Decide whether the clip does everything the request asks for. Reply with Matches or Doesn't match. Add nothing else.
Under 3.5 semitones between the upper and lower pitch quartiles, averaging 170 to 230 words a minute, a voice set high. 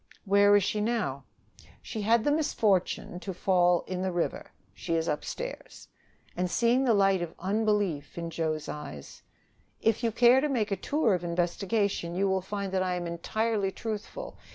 Doesn't match